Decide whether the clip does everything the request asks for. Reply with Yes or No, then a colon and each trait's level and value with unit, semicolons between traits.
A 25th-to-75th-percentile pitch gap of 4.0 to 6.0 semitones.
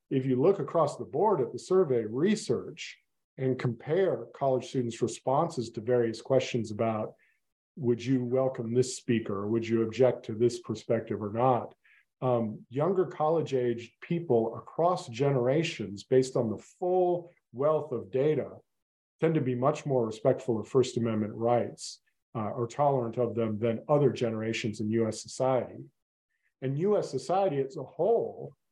No: average, 3.0 semitones